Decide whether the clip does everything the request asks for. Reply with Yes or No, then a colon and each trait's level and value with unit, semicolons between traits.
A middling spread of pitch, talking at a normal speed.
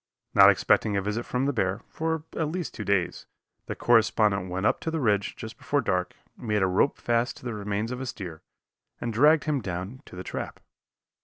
No: average, 4.9 semitones; fast, 210 wpm